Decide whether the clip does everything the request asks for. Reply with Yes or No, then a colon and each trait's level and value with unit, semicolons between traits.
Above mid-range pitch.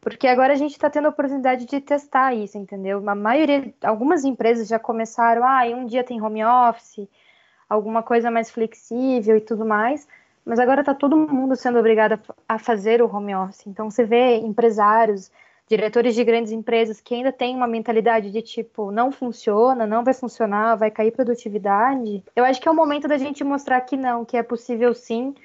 Yes: high, 235 Hz